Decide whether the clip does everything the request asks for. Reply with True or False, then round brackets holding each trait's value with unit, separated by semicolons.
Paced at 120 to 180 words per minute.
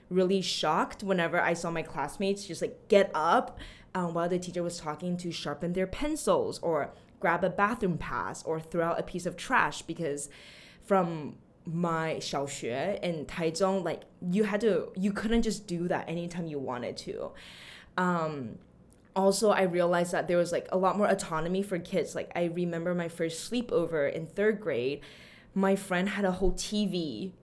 True (175 wpm)